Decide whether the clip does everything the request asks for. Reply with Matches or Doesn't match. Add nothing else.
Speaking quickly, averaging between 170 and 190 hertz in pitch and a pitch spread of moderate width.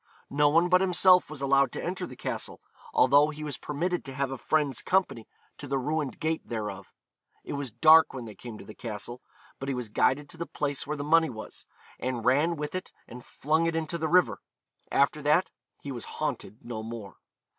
Doesn't match